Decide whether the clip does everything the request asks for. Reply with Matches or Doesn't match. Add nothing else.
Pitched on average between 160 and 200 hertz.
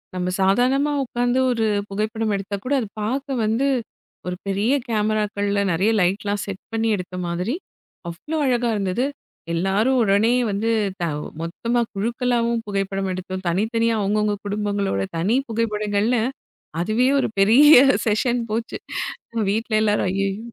Doesn't match